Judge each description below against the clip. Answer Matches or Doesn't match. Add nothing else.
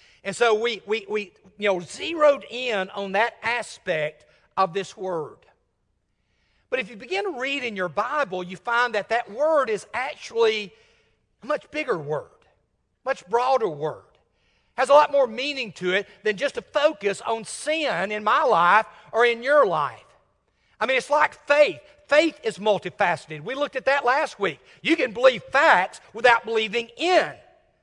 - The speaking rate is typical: Matches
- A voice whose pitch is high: Matches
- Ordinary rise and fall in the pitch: Doesn't match